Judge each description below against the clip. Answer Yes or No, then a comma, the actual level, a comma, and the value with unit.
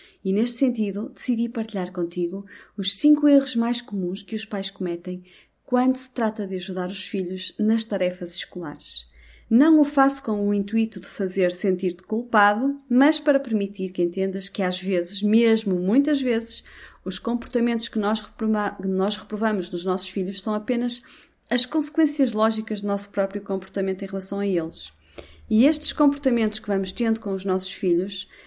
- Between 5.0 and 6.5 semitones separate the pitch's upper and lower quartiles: No, average, 3.9 semitones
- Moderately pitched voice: No, high, 205 Hz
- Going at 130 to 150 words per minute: No, average, 165 wpm